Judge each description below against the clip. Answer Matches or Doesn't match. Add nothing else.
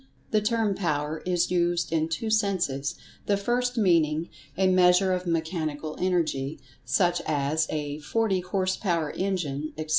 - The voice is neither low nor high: Matches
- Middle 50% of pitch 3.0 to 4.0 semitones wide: Matches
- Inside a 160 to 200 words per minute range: Doesn't match